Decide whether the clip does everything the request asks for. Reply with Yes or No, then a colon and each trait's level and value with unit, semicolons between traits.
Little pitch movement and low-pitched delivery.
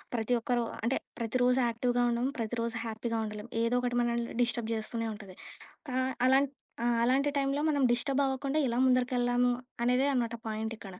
No: narrow, 1.7 semitones; high, 240 Hz